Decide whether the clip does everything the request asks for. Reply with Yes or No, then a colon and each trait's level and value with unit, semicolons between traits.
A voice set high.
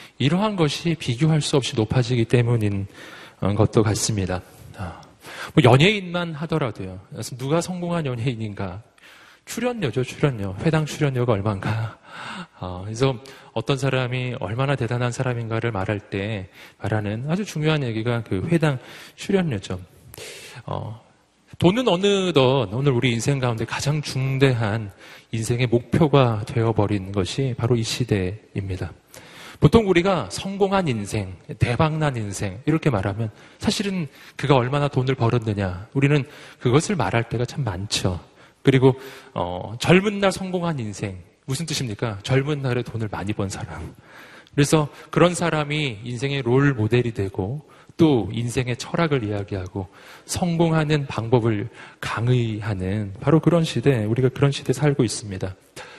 No: low, 125 Hz